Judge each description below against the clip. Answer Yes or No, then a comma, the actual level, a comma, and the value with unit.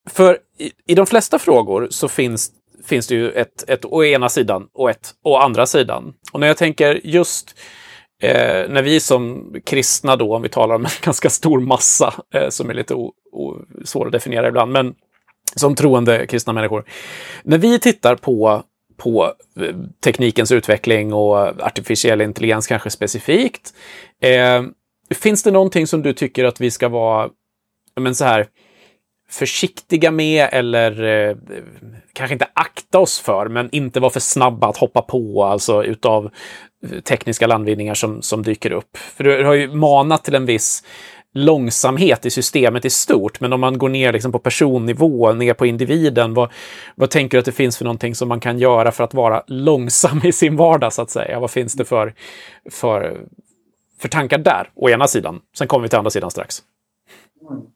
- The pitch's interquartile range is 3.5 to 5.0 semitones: Yes, average, 4.0 semitones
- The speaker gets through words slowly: No, average, 175 wpm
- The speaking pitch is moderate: No, low, 125 Hz